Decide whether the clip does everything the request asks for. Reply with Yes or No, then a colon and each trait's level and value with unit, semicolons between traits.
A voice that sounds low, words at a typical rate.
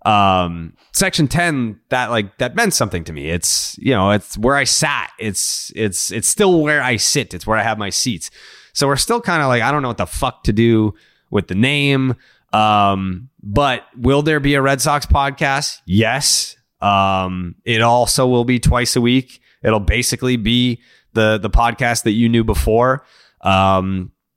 Yes: low, 120 Hz; average, 185 wpm